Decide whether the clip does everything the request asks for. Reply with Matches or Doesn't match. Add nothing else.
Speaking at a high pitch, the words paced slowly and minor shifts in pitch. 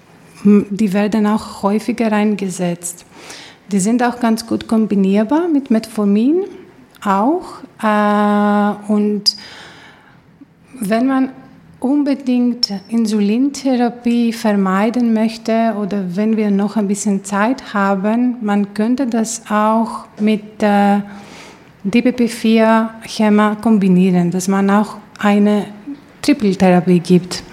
Matches